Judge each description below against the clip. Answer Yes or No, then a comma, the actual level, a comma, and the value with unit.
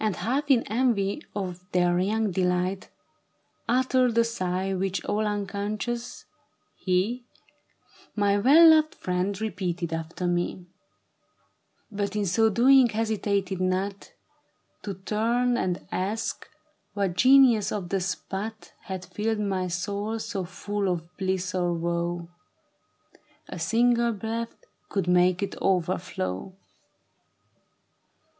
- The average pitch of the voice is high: Yes, high, 200 Hz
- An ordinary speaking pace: No, slow, 120 wpm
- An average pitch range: Yes, average, 3.5 semitones